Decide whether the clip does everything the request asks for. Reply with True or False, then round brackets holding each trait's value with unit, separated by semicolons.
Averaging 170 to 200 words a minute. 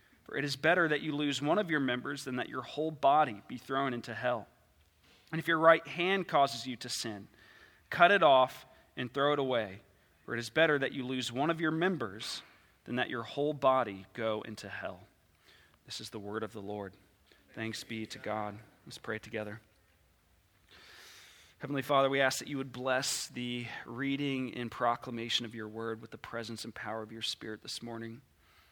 True (195 wpm)